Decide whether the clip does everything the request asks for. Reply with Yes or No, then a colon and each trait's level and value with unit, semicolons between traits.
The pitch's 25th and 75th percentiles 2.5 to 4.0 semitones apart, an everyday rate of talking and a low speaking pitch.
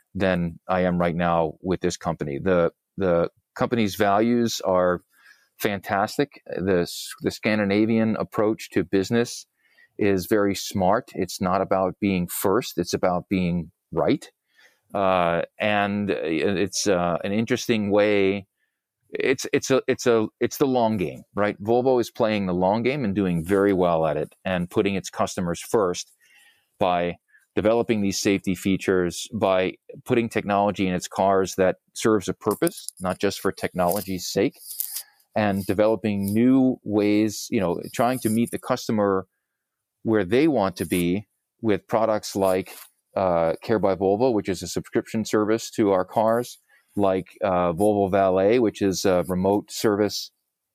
Yes: average, 3.0 semitones; average, 150 wpm; low, 100 Hz